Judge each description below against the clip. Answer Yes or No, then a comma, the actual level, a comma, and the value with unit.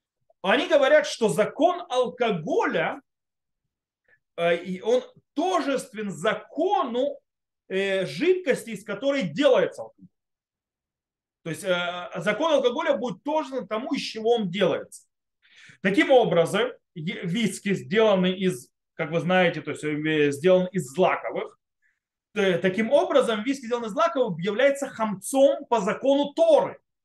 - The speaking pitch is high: Yes, high, 225 Hz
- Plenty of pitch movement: Yes, wide, 7.3 semitones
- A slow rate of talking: Yes, slow, 105 wpm